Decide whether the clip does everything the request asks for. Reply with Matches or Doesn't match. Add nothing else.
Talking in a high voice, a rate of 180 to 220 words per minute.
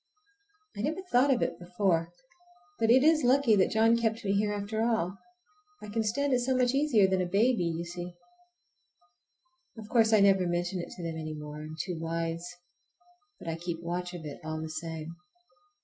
Matches